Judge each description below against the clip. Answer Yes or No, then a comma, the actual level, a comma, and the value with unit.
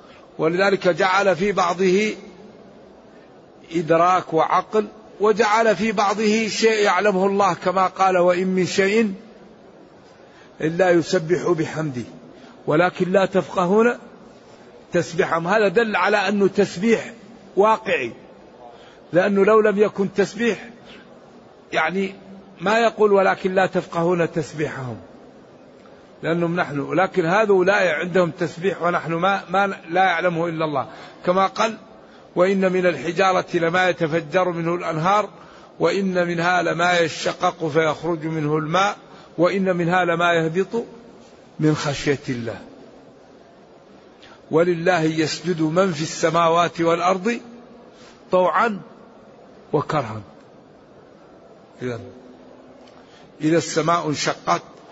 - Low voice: No, medium, 180 Hz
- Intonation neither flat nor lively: Yes, average, 3.1 semitones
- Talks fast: No, average, 100 wpm